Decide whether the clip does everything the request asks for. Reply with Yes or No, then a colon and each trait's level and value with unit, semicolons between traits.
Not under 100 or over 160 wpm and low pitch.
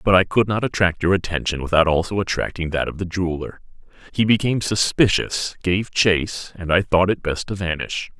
No: average, 190 wpm; very low, 90 Hz